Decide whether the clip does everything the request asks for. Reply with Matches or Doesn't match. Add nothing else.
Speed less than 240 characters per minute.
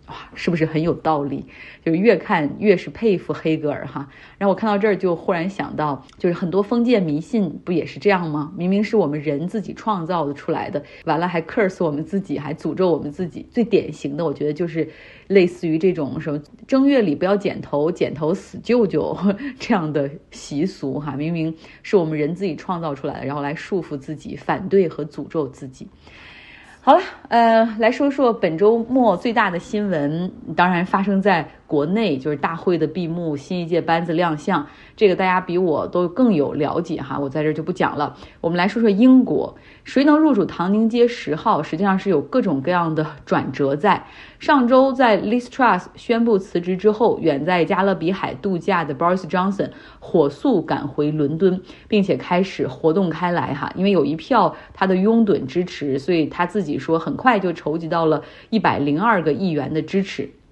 Doesn't match